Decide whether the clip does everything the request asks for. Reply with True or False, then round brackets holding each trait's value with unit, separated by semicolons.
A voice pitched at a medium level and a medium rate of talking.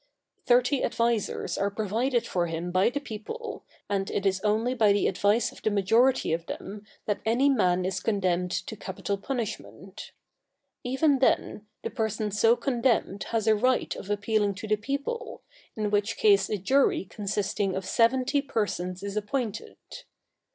False (210 Hz; 160 wpm)